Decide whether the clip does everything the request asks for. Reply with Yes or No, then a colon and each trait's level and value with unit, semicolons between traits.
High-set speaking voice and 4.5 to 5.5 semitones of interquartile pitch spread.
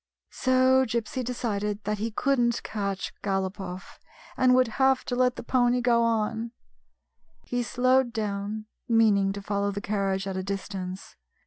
No: high, 220 Hz; average, 3.7 semitones